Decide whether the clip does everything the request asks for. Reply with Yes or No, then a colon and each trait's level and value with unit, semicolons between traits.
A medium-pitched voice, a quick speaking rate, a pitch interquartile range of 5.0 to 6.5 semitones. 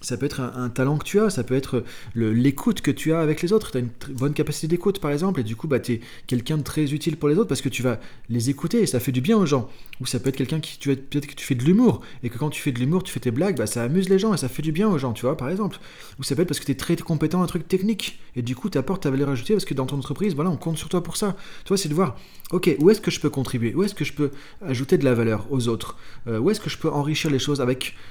Yes: medium, 145 Hz; fast, 350 wpm; wide, 5.5 semitones